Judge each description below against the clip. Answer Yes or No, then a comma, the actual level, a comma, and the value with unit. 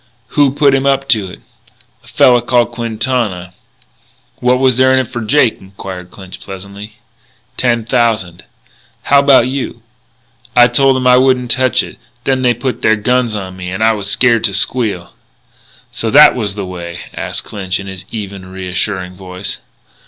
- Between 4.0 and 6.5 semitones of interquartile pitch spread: Yes, average, 5.0 semitones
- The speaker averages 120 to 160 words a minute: No, average, 170 wpm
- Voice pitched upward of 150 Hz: No, low, 115 Hz